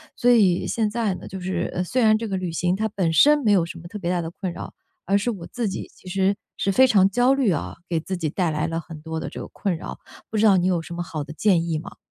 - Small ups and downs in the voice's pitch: No, average, 3.9 semitones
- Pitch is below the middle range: No, medium, 185 Hz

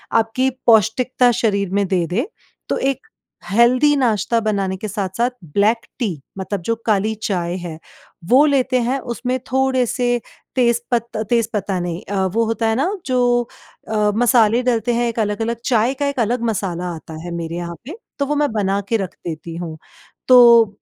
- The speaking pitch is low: No, high, 225 Hz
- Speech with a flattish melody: No, average, 4.1 semitones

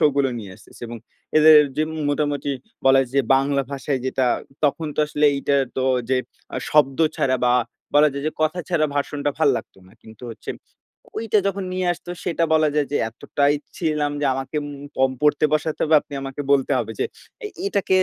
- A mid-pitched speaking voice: Yes, medium, 145 Hz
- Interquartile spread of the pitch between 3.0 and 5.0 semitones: No, narrow, 2.4 semitones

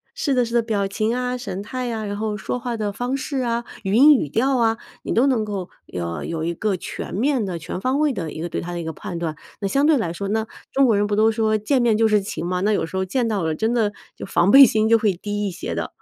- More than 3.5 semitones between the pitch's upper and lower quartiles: Yes, average, 4.1 semitones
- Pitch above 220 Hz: No, high, 215 Hz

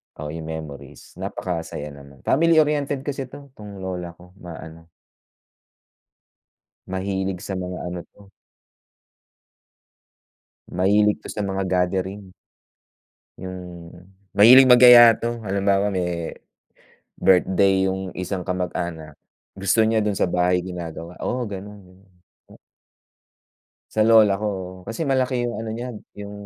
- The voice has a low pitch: Yes, very low, 95 Hz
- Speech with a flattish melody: No, average, 3.5 semitones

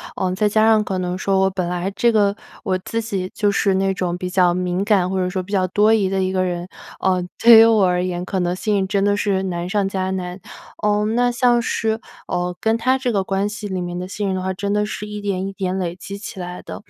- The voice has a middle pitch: No, high, 195 Hz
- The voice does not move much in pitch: Yes, narrow, 2.3 semitones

